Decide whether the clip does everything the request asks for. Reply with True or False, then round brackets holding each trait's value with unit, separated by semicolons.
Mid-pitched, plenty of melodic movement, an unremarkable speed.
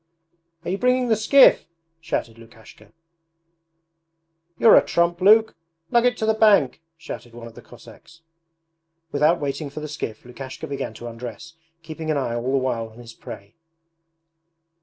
True (150 Hz; 7.7 semitones; 160 wpm)